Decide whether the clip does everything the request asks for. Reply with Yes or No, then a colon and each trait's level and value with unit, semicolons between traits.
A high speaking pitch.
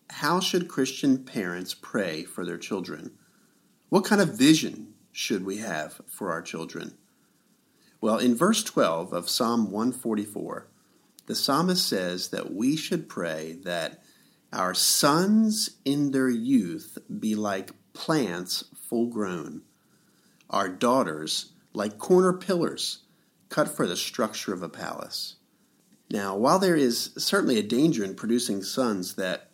No: medium, 140 Hz